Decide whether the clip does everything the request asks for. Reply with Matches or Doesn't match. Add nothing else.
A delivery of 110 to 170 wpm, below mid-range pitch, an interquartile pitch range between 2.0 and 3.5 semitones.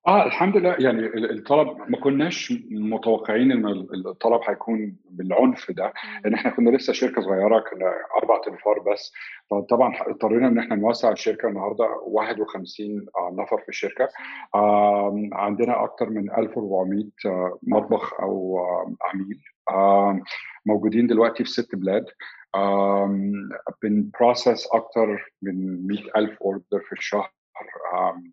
Matches